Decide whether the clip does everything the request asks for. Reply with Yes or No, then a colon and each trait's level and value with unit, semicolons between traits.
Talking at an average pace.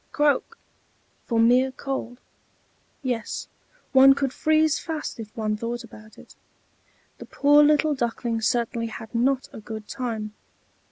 No: slow, 130 wpm